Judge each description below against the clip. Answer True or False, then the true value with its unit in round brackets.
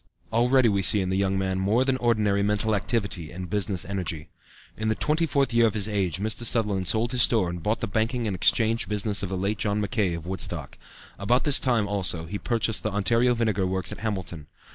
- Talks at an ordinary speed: False (220 wpm)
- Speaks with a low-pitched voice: True (105 Hz)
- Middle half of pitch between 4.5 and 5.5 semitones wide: False (3.2 semitones)